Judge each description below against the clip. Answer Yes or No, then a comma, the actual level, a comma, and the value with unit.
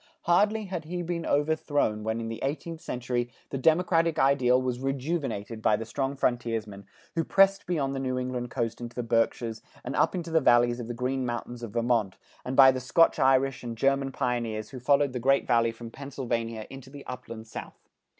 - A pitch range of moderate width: Yes, average, 3.3 semitones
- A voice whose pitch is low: Yes, low, 125 Hz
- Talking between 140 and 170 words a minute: No, average, 190 wpm